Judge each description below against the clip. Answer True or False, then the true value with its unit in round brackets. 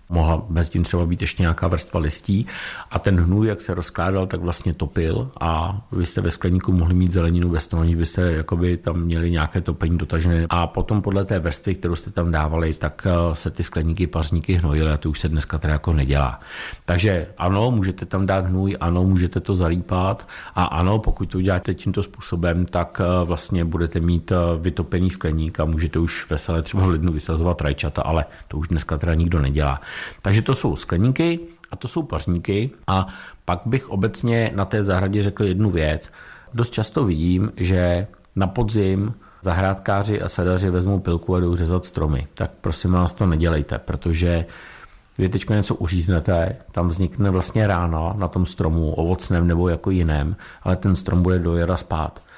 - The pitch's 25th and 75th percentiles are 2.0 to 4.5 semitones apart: True (2.5 semitones)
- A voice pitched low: True (90 Hz)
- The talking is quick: True (180 wpm)